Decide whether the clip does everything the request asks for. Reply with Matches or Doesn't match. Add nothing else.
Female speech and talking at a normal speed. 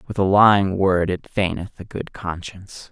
Doesn't match